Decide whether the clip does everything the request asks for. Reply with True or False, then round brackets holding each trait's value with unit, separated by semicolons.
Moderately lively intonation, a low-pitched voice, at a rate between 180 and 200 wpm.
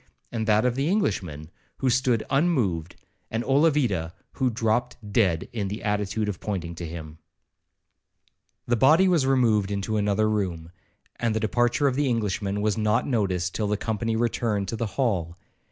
False (4.0 semitones; 110 Hz; 165 wpm)